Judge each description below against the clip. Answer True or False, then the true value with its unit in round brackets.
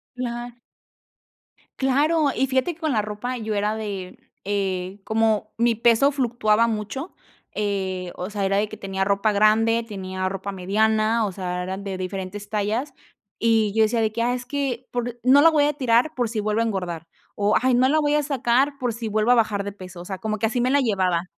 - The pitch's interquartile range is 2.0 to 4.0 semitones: True (3.6 semitones)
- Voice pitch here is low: False (220 Hz)